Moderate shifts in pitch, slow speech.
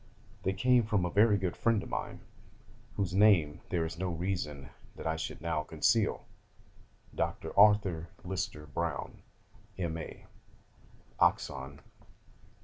Yes: average, 3.9 semitones; slow, 125 wpm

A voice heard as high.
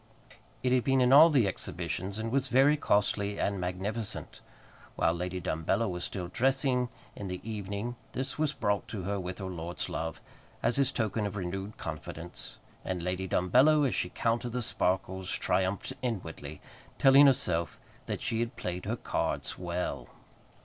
No: low, 100 Hz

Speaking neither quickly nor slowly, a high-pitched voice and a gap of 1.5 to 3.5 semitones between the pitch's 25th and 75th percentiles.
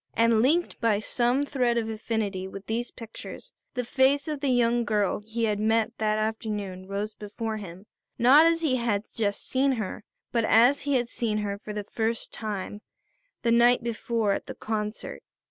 Yes: average, 180 wpm; high, 225 Hz; narrow, 2.5 semitones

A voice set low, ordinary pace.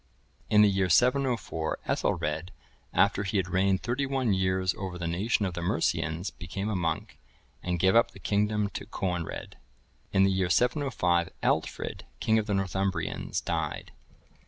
Yes: very low, 95 Hz; average, 170 wpm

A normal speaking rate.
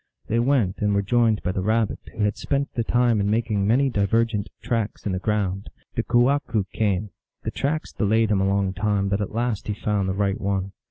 No: fast, 215 wpm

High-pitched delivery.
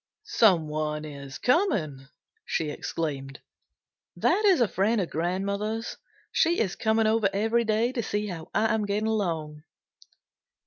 Yes: high, 200 Hz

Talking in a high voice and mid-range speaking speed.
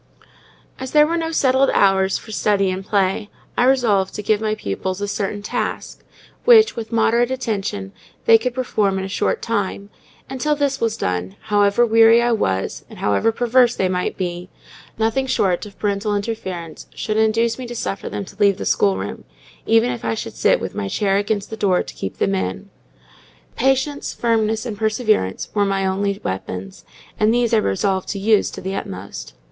Yes: high, 210 Hz; average, 185 wpm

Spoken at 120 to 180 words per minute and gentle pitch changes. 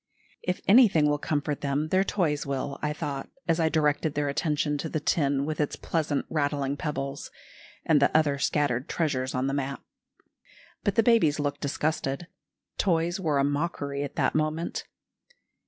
Yes: average, 165 wpm; narrow, 2.2 semitones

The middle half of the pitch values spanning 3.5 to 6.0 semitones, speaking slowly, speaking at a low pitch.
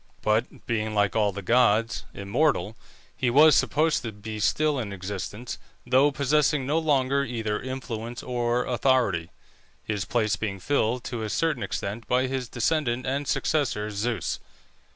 No: average, 3.8 semitones; average, 150 wpm; low, 120 Hz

